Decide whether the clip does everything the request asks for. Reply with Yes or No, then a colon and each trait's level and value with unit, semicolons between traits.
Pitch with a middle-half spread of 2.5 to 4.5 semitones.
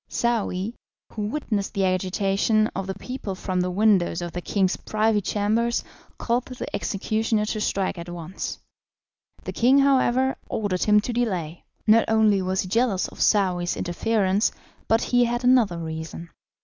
Yes: average, 3.7 semitones